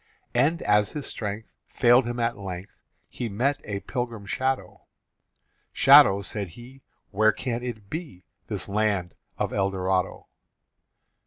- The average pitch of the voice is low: Yes, low, 110 Hz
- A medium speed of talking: No, slow, 130 wpm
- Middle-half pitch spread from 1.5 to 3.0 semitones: No, average, 3.7 semitones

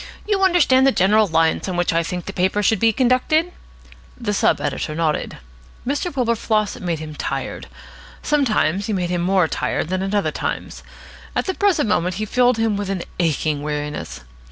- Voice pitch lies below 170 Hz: No, high, 200 Hz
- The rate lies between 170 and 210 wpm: Yes, average, 180 wpm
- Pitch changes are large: Yes, wide, 6.3 semitones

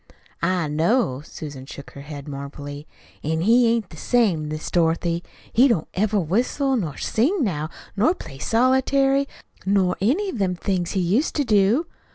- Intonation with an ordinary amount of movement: No, wide, 7.8 semitones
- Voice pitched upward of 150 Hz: Yes, high, 190 Hz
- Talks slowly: No, average, 165 wpm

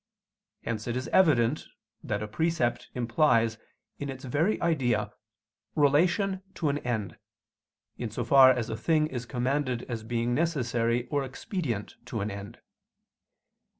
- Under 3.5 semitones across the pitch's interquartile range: No, average, 4.5 semitones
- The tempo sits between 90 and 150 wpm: Yes, average, 140 wpm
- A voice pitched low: Yes, low, 125 Hz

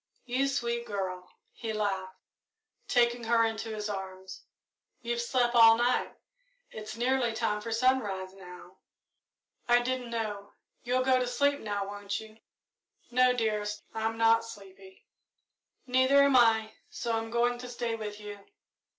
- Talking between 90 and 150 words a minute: Yes, average, 140 wpm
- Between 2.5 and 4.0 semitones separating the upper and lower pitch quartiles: Yes, average, 2.8 semitones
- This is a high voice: Yes, high, 225 Hz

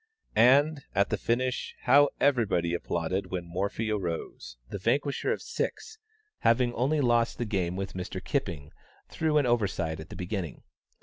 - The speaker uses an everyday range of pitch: No, wide, 6.4 semitones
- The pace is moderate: Yes, average, 150 wpm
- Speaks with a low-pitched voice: Yes, low, 110 Hz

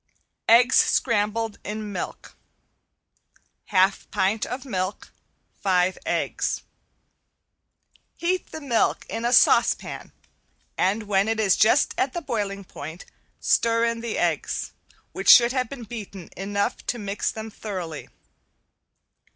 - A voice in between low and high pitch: No, high, 215 Hz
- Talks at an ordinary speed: No, slow, 120 wpm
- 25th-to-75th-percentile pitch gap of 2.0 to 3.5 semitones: Yes, average, 3.2 semitones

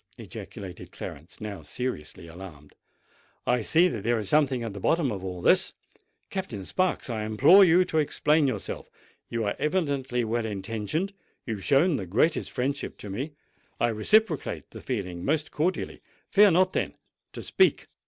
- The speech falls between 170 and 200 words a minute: No, average, 155 wpm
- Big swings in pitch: Yes, wide, 7.5 semitones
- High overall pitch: No, low, 125 Hz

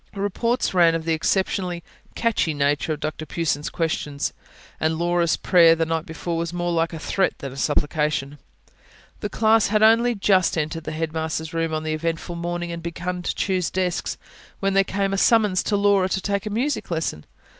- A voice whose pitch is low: No, medium, 170 Hz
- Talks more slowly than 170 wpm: No, average, 190 wpm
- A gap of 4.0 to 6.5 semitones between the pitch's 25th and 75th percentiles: No, average, 3.4 semitones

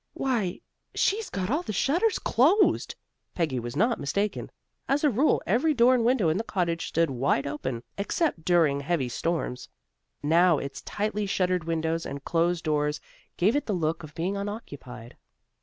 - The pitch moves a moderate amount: No, wide, 7.0 semitones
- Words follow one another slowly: No, average, 165 wpm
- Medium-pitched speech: Yes, medium, 175 Hz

